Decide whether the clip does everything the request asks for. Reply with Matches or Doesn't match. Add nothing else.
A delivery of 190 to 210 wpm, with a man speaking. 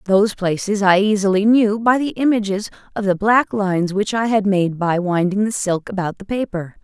Doesn't match